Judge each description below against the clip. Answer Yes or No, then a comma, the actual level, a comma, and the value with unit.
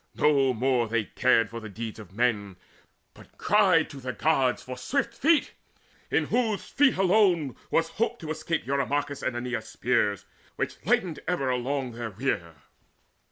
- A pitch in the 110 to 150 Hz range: Yes, low, 135 Hz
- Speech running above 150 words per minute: Yes, average, 160 wpm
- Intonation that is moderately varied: No, wide, 6.0 semitones